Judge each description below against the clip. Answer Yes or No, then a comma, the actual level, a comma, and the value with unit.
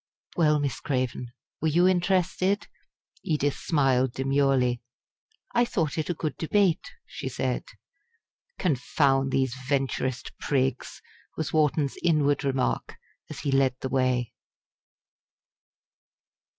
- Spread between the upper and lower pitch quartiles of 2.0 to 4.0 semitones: Yes, average, 3.2 semitones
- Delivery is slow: Yes, slow, 110 wpm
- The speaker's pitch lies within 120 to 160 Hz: Yes, medium, 140 Hz